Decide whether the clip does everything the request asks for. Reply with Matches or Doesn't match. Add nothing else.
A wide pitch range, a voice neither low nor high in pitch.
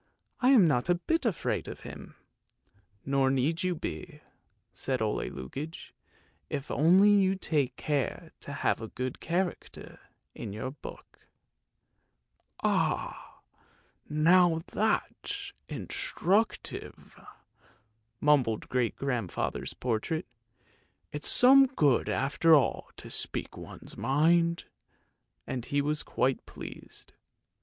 Matches